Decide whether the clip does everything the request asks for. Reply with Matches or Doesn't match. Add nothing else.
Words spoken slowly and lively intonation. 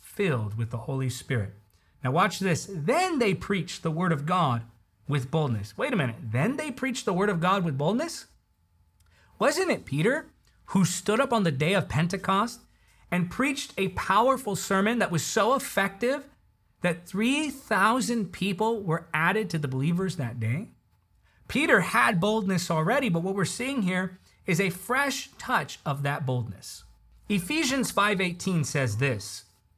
Doesn't match